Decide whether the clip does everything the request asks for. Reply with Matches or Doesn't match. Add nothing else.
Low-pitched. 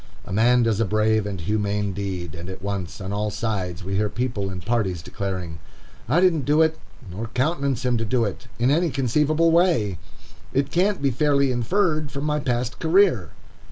Matches